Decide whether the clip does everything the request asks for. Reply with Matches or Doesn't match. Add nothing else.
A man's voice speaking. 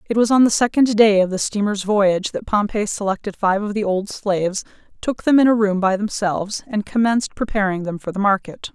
Doesn't match